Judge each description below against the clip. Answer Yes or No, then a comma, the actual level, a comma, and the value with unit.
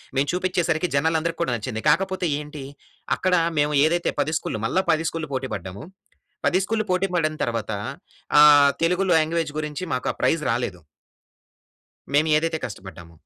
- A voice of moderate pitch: Yes, medium, 155 Hz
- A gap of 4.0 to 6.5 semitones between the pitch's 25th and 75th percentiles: Yes, average, 4.5 semitones